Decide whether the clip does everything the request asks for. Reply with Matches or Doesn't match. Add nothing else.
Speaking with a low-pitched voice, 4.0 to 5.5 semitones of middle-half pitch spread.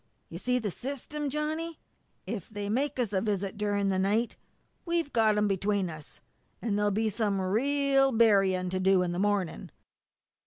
Doesn't match